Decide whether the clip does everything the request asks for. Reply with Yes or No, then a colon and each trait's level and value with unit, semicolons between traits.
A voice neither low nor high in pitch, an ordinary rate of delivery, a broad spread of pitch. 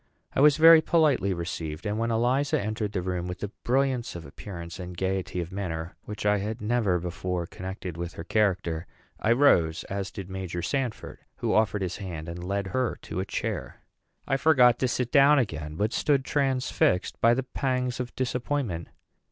No: low, 105 Hz; average, 185 wpm; wide, 6.1 semitones